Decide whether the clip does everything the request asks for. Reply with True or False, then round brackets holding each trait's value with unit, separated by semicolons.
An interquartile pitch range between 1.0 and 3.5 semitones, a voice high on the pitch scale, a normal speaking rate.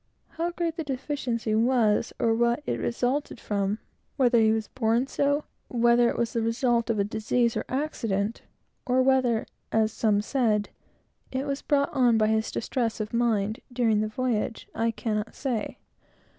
True (2.9 semitones; 235 Hz; 160 wpm)